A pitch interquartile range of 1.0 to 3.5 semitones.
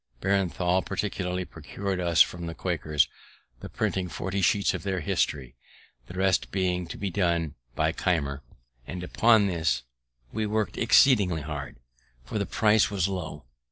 Yes: average, 3.2 semitones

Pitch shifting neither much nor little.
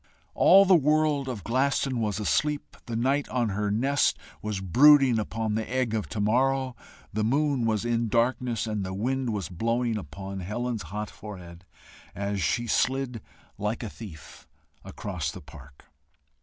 Yes: average, 4.1 semitones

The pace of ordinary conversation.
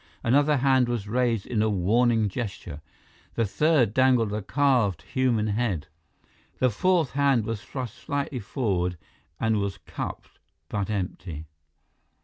No: slow, 130 wpm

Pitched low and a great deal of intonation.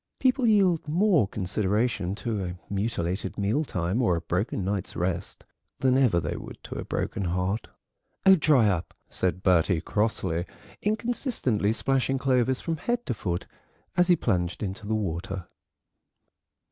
Yes: low, 105 Hz; wide, 6.8 semitones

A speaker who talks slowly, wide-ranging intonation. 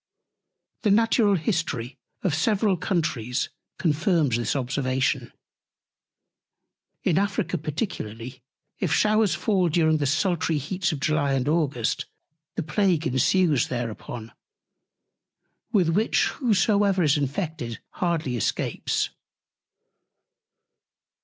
Yes: slow, 95 wpm; wide, 6.0 semitones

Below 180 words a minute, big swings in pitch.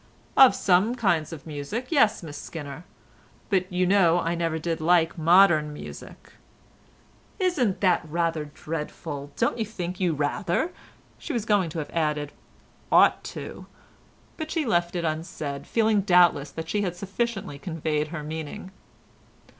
No: average, 140 wpm; average, 4.3 semitones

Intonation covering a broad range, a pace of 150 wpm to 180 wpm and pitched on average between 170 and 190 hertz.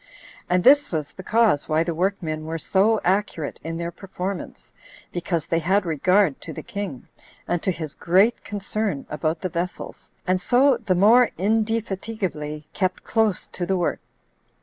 No: average, 4.0 semitones; average, 160 wpm; medium, 185 Hz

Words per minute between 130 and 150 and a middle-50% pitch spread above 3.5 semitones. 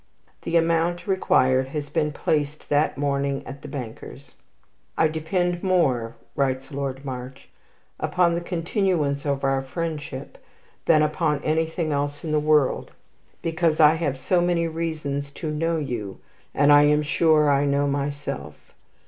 No: average, 145 wpm; average, 2.9 semitones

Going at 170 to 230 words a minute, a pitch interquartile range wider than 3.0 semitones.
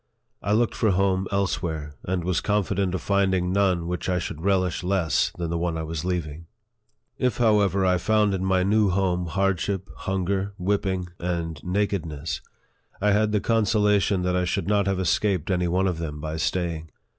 No: average, 190 wpm; narrow, 2.5 semitones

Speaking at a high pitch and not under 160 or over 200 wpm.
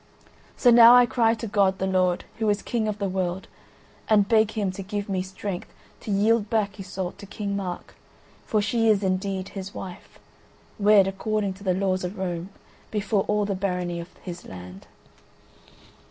Yes: high, 200 Hz; average, 180 wpm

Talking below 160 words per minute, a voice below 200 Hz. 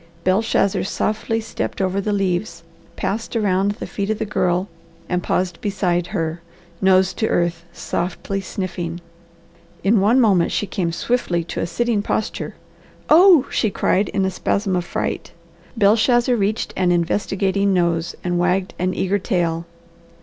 Yes: average, 150 wpm; high, 190 Hz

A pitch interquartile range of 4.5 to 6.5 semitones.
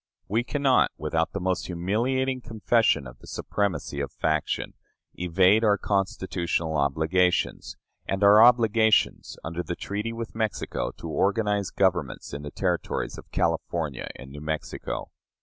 Yes: average, 5.3 semitones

